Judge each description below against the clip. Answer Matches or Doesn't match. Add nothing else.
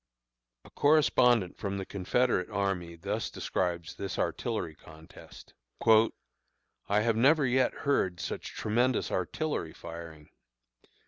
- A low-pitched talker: Matches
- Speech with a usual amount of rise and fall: Doesn't match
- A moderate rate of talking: Doesn't match